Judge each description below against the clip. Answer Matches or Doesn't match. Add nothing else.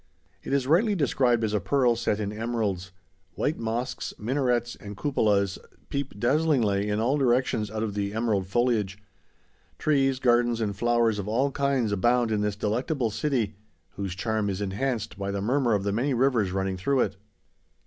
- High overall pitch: Doesn't match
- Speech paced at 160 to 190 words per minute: Matches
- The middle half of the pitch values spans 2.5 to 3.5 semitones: Doesn't match